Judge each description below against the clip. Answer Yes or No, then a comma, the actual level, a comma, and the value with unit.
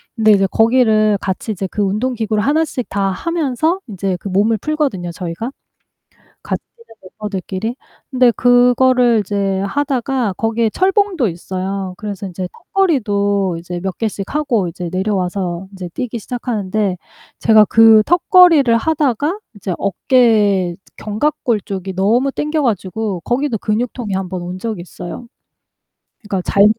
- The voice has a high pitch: Yes, high, 215 Hz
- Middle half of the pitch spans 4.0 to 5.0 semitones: Yes, average, 4.6 semitones